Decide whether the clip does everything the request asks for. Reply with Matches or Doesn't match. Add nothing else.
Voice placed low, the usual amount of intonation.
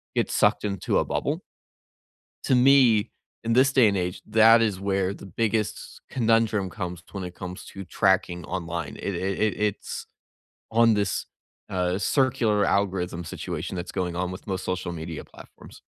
Matches